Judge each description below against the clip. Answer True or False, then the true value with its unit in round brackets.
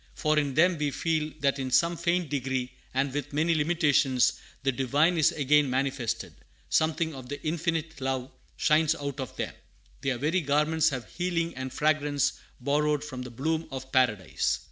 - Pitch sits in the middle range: True (145 Hz)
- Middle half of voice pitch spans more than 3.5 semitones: False (3.1 semitones)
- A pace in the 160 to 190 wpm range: True (165 wpm)